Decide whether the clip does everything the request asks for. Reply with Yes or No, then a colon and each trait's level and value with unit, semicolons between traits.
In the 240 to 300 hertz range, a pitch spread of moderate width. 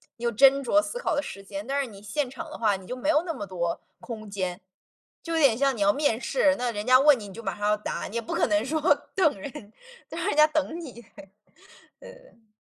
No: high, 245 Hz; wide, 6.1 semitones